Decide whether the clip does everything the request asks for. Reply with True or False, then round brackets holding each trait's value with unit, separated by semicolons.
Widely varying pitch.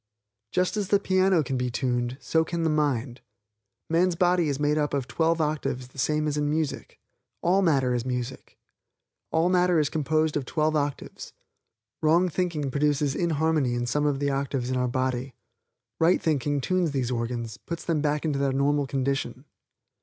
False (3.6 semitones)